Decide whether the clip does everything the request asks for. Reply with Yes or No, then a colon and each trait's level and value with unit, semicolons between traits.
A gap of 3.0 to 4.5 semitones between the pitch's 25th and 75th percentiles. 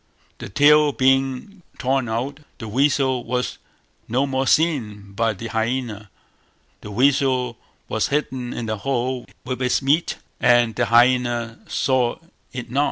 No: narrow, 2.5 semitones